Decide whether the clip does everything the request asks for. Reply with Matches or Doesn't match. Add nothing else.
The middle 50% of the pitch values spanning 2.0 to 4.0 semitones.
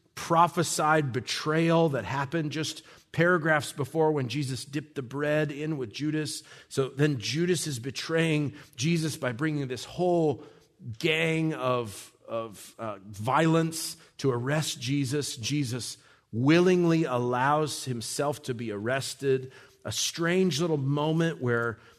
Matches